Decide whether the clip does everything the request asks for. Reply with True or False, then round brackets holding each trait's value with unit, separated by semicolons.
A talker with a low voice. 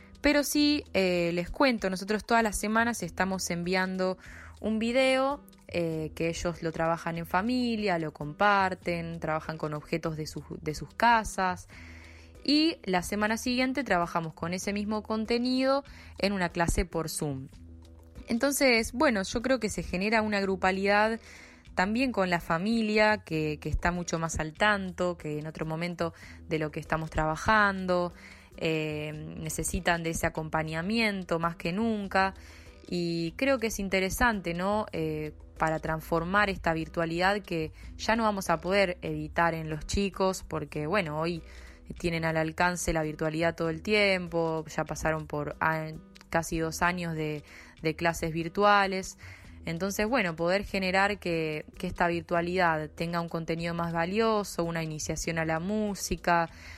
False (175 Hz)